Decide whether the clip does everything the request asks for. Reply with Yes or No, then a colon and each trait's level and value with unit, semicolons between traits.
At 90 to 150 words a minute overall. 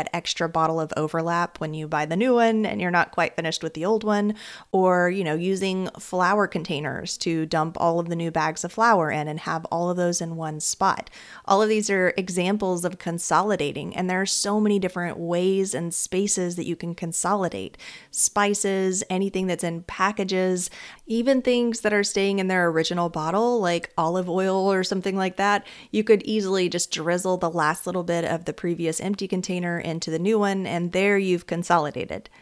No: average, 200 wpm